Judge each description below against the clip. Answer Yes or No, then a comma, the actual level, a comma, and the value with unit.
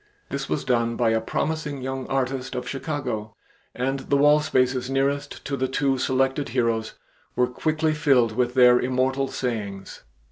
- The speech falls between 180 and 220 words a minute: No, average, 155 wpm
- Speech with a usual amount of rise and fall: No, narrow, 2.0 semitones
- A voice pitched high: No, low, 130 Hz